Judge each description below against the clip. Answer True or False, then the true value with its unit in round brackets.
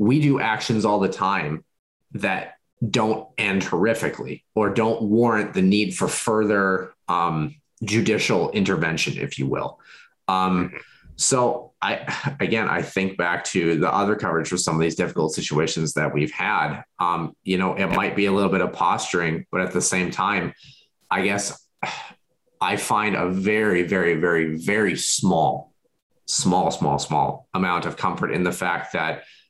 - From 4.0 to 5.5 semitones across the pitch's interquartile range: False (3.4 semitones)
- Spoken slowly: False (160 wpm)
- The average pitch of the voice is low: True (100 Hz)